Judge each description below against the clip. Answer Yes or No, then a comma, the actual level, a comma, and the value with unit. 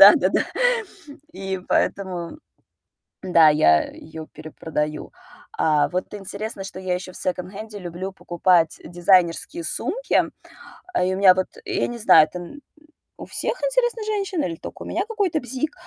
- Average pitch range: No, wide, 6.3 semitones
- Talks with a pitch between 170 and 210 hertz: Yes, medium, 185 Hz